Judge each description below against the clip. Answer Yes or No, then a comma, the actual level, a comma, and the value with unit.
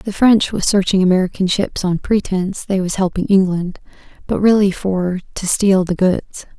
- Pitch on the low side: No, high, 190 Hz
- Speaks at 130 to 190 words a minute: Yes, average, 175 wpm